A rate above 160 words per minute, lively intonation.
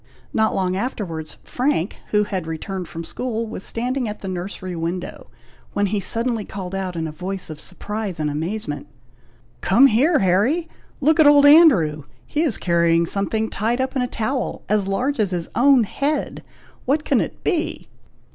Yes: average, 175 wpm; wide, 6.1 semitones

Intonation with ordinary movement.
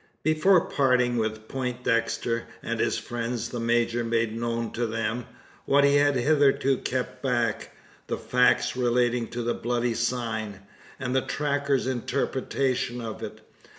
No: narrow, 2.2 semitones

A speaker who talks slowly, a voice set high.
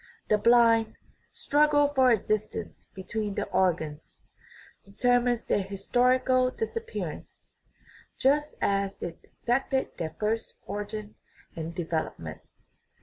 Yes: slow, 110 wpm; high, 220 Hz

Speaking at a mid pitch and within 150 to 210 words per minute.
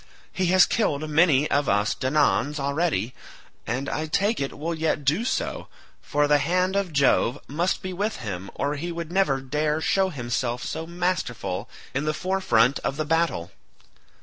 Yes: medium, 150 Hz; average, 170 wpm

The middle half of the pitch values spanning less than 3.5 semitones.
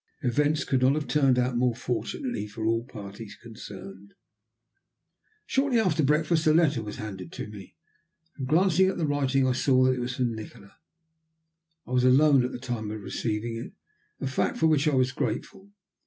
No: average, 4.9 semitones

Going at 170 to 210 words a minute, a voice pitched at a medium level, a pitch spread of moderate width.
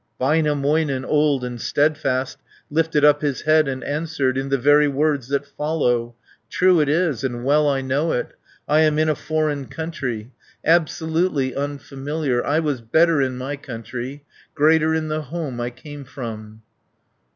No: average, 160 wpm; medium, 145 Hz; average, 3.1 semitones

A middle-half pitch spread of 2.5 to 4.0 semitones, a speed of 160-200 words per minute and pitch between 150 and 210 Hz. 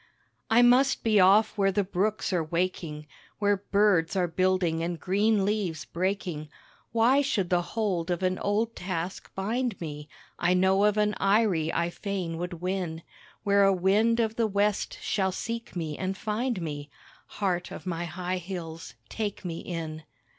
Yes: average, 3.4 semitones; average, 165 wpm; high, 190 Hz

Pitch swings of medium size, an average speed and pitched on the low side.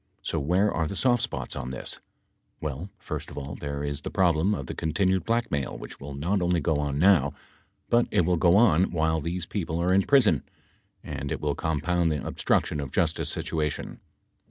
Yes: average, 4.2 semitones; average, 195 wpm; very low, 80 Hz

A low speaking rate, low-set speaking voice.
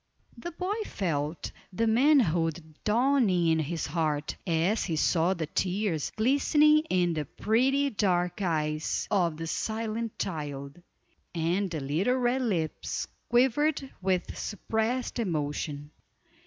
No: slow, 120 wpm; medium, 185 Hz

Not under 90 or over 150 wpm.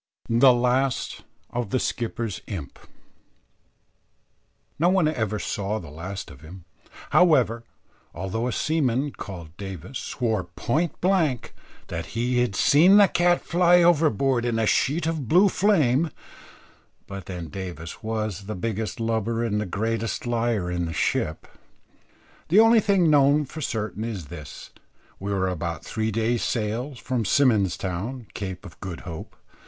Yes: average, 145 wpm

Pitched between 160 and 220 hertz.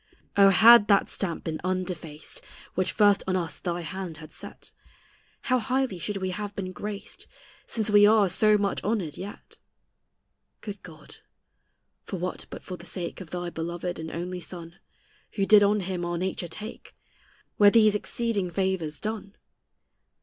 Yes: high, 190 Hz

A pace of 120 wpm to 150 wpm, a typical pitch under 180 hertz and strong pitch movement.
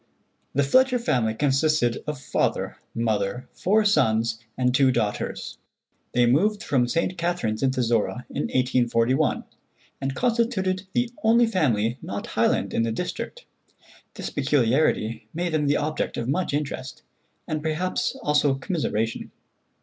Yes: slow, 135 wpm; medium, 140 Hz; wide, 6.9 semitones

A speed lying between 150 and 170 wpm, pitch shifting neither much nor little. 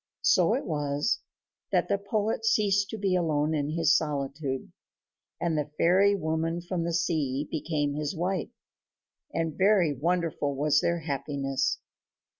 No: average, 140 wpm; average, 3.6 semitones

